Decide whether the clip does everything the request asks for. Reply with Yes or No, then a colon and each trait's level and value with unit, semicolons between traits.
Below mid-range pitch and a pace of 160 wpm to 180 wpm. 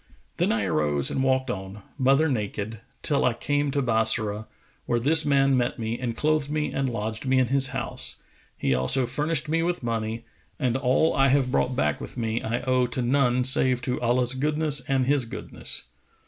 No: low, 125 Hz; average, 190 wpm